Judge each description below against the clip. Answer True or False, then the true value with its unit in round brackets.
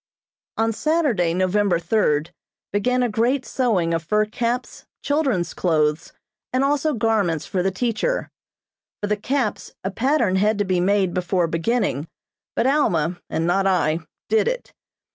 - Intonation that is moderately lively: False (5.8 semitones)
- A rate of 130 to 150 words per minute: True (145 wpm)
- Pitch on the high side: True (205 Hz)